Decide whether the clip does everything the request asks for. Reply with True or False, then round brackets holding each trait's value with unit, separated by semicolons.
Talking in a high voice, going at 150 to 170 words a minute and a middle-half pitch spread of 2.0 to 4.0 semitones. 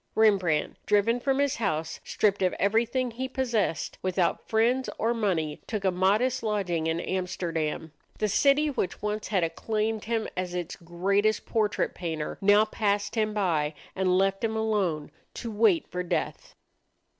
True (205 Hz; 155 wpm; 3.7 semitones)